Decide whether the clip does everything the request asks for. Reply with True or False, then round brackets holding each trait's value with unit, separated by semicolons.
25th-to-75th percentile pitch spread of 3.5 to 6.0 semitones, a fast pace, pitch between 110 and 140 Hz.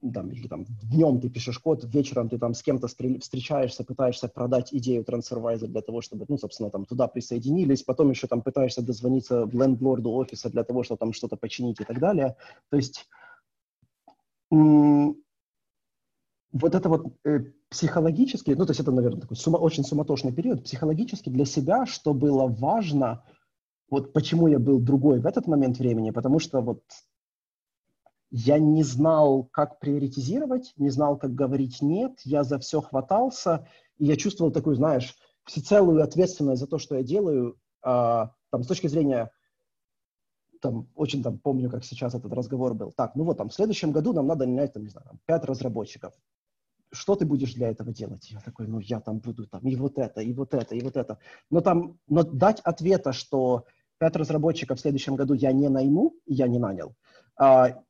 True (3.8 semitones; 175 wpm; 135 Hz)